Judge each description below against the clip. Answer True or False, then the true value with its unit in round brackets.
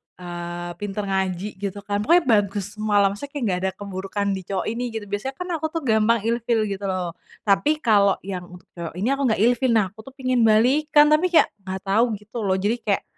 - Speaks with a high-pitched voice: True (205 Hz)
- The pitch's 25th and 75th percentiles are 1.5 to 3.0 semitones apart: False (3.5 semitones)